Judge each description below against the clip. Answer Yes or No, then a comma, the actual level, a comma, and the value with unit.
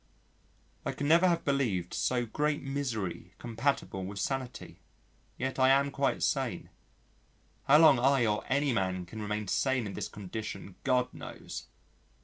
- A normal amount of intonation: Yes, average, 5.0 semitones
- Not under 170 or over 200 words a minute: No, average, 145 wpm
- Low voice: Yes, low, 125 Hz